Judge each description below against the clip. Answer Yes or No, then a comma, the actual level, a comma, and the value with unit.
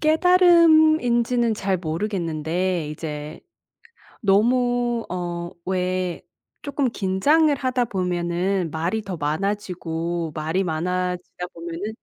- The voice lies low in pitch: No, medium, 185 Hz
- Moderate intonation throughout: No, wide, 5.7 semitones